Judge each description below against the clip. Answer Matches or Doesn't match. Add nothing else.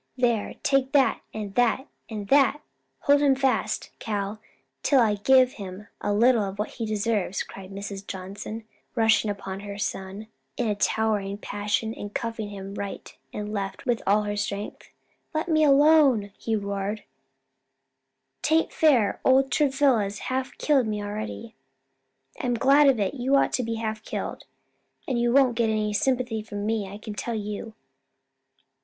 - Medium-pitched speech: Doesn't match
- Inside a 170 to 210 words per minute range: Doesn't match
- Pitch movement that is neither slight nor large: Matches